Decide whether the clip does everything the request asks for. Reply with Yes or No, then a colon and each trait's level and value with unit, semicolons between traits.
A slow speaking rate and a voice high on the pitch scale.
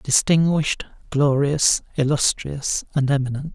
No: slow, 85 wpm; medium, 145 Hz